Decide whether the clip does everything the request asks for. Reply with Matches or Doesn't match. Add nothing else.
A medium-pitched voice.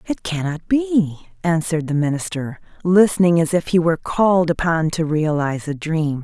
Matches